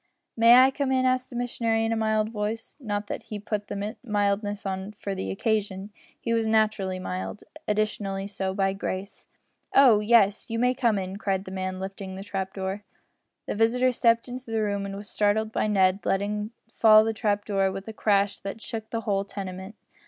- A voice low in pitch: No, high, 210 Hz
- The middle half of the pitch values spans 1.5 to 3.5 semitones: Yes, narrow, 2.4 semitones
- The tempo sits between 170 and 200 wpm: Yes, average, 195 wpm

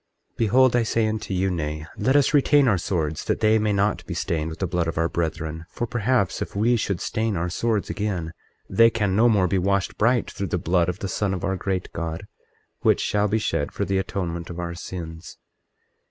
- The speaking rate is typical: No, fast, 220 wpm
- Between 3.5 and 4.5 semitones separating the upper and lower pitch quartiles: Yes, average, 4.2 semitones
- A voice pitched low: Yes, very low, 95 Hz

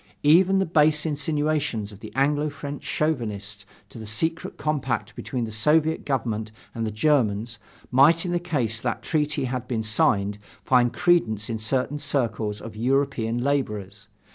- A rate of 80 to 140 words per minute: No, average, 150 wpm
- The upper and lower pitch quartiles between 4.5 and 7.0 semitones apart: Yes, wide, 5.6 semitones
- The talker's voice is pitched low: Yes, low, 130 Hz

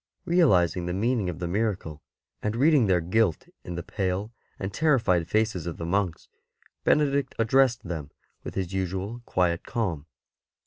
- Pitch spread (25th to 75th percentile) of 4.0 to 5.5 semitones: Yes, average, 4.8 semitones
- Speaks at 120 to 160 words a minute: Yes, average, 150 wpm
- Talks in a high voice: No, very low, 95 Hz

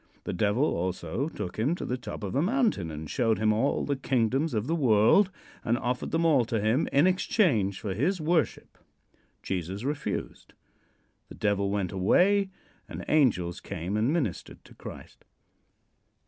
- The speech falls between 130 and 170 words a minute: Yes, average, 160 wpm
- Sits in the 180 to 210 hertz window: No, low, 120 Hz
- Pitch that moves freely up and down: Yes, wide, 7.4 semitones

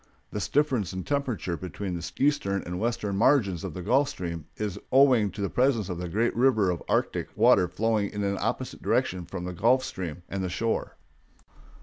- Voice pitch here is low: Yes, low, 100 Hz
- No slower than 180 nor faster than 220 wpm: Yes, average, 195 wpm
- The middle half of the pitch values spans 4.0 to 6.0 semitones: Yes, average, 4.7 semitones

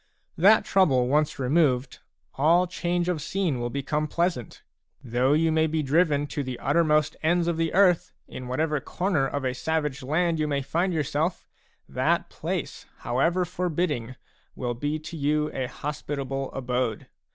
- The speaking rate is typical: Yes, average, 155 wpm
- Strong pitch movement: No, average, 4.1 semitones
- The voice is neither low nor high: Yes, medium, 150 Hz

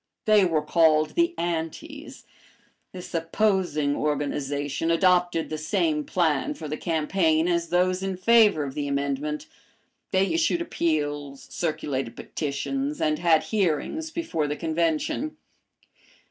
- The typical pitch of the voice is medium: Yes, medium, 165 Hz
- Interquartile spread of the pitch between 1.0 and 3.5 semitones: No, average, 3.9 semitones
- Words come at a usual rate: No, slow, 120 wpm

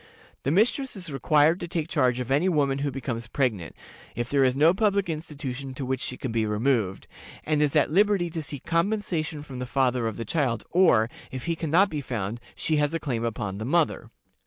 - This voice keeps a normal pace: No, fast, 215 wpm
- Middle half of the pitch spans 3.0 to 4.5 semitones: No, average, 4.9 semitones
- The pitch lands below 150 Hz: Yes, medium, 140 Hz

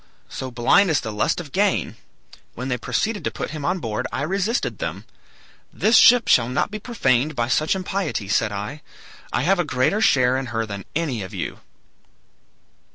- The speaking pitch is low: No, medium, 145 Hz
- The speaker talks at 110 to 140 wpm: No, average, 185 wpm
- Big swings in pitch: Yes, wide, 8.0 semitones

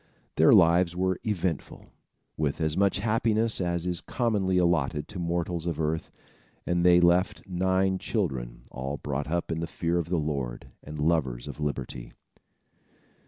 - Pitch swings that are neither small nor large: Yes, average, 3.5 semitones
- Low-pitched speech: Yes, very low, 85 Hz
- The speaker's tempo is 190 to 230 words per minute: No, average, 155 wpm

